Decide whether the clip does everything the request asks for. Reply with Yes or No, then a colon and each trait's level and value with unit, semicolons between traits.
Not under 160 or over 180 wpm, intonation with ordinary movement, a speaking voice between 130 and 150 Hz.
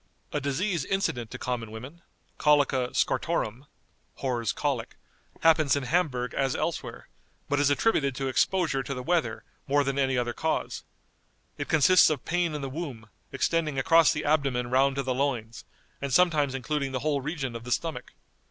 Yes: average, 170 wpm; average, 3.4 semitones; medium, 140 Hz